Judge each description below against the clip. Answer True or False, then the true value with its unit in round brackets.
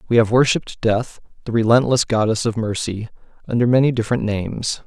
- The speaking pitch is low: True (115 Hz)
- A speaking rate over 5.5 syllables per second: True (6.0 syllables/s)